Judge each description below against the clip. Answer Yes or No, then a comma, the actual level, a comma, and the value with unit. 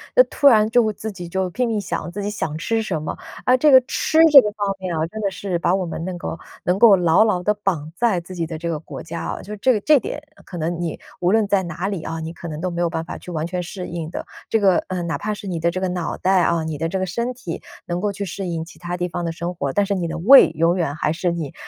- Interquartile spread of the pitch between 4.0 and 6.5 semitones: No, average, 3.6 semitones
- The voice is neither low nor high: Yes, medium, 180 Hz